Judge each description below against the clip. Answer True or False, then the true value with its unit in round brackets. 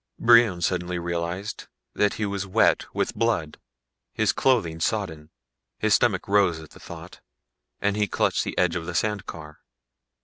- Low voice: True (95 Hz)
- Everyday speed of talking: True (160 wpm)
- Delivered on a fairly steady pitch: False (3.7 semitones)